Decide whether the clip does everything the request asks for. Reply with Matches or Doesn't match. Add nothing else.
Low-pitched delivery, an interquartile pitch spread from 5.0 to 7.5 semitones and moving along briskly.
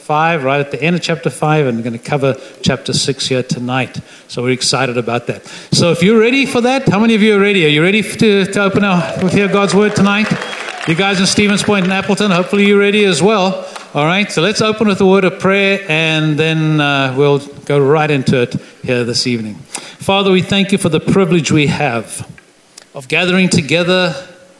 Doesn't match